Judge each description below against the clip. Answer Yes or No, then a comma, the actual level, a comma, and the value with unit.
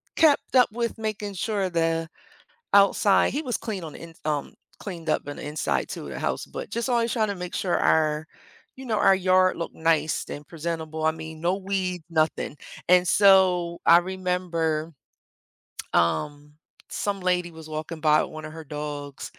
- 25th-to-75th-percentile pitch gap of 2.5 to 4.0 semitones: Yes, average, 3.7 semitones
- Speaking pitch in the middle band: Yes, medium, 170 Hz